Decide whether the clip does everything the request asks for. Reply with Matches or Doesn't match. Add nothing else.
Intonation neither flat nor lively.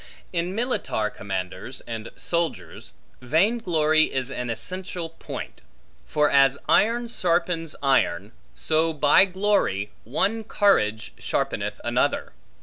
Doesn't match